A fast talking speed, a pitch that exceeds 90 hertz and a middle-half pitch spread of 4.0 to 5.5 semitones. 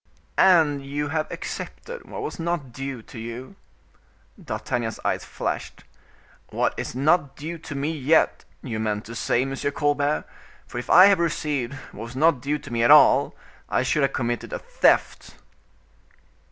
No: average, 165 wpm; medium, 140 Hz; average, 4.3 semitones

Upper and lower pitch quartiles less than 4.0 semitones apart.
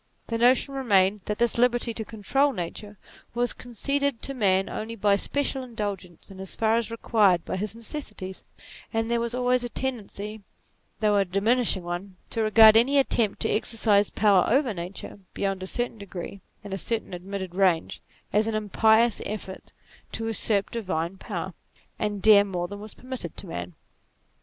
Yes: average, 3.3 semitones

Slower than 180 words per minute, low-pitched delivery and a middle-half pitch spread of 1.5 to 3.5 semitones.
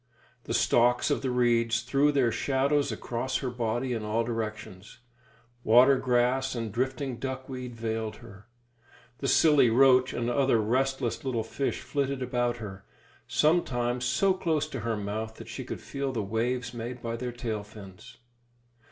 Yes: average, 160 wpm; low, 120 Hz; narrow, 2.6 semitones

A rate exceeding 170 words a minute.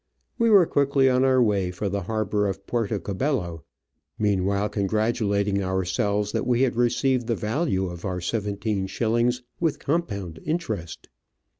No: average, 150 wpm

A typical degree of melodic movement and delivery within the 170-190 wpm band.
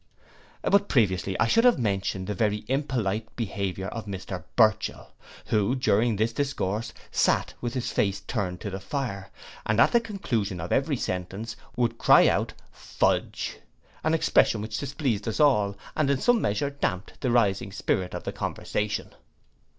No: average, 5.0 semitones; average, 160 wpm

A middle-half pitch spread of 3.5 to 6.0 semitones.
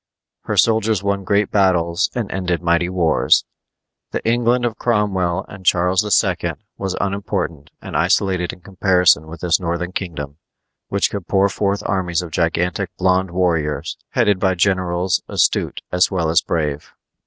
No: narrow, 2.5 semitones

